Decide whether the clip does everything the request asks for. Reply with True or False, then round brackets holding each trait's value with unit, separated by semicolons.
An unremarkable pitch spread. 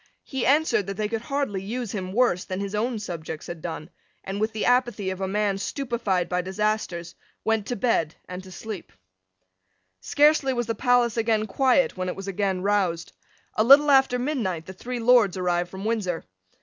True (4.6 semitones)